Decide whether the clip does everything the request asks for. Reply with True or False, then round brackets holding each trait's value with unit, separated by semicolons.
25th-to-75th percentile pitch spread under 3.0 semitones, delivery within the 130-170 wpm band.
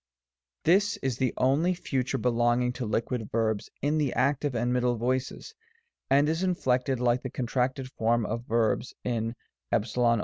True (2.4 semitones; 165 wpm)